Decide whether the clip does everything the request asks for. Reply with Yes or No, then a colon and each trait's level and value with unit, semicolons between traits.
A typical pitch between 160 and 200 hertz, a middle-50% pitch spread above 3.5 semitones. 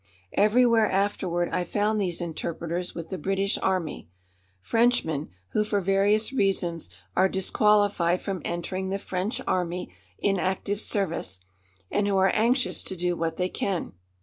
No: high, 190 Hz; average, 2.8 semitones